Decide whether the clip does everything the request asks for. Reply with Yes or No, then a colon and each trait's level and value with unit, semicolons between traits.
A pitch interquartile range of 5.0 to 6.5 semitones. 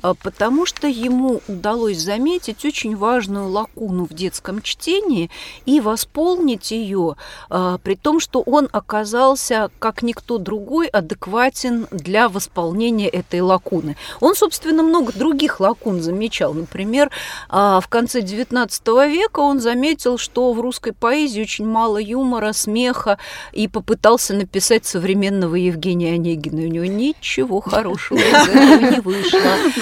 Yes: average, 5.3 semitones